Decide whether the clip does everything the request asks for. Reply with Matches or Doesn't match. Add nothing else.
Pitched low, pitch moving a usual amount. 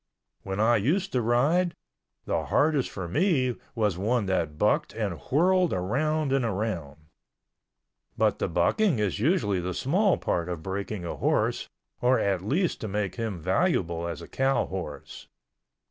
Doesn't match